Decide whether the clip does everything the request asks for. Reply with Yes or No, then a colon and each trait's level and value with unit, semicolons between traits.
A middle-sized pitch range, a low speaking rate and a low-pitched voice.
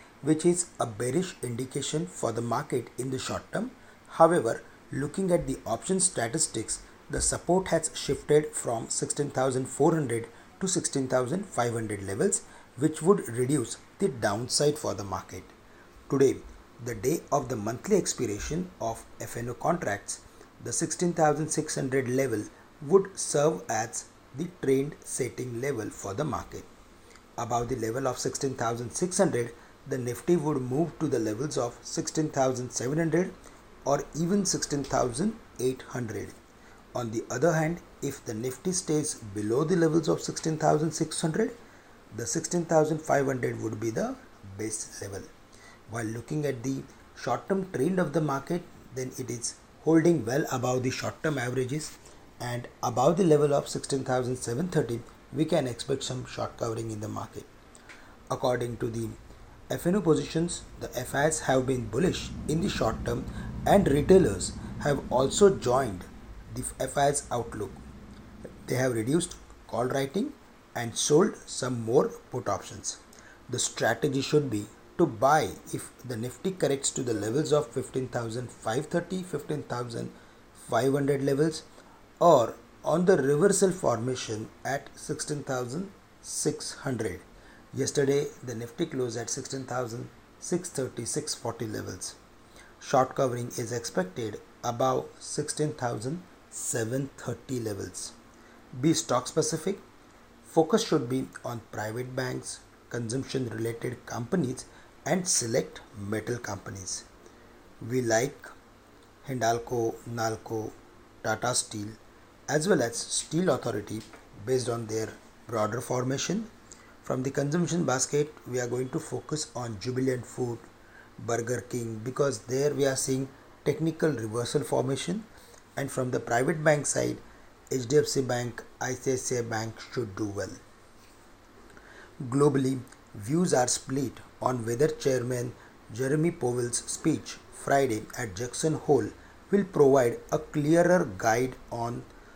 Yes: average, 4.6 semitones; slow, 120 wpm; low, 130 Hz